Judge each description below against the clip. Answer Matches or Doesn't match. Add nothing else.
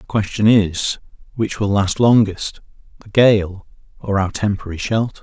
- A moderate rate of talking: Matches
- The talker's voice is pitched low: Matches